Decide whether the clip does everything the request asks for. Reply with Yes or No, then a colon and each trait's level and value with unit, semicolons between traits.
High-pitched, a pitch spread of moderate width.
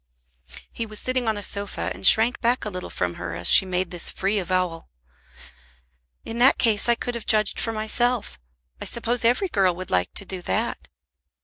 Yes: high, 210 Hz; average, 4.4 semitones